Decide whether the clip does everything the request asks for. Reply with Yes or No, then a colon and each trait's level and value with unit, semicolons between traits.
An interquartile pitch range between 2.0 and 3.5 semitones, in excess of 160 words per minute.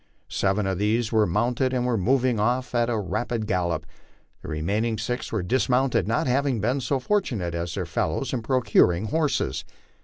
No: average, 4.4 semitones; average, 175 wpm